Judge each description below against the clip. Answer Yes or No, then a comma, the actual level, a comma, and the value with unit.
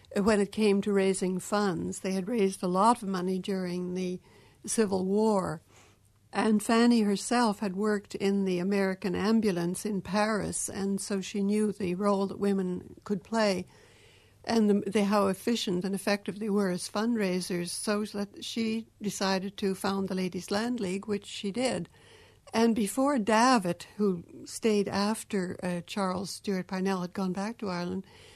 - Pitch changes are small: Yes, narrow, 2.0 semitones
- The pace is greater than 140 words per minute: Yes, average, 160 wpm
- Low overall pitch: No, high, 200 Hz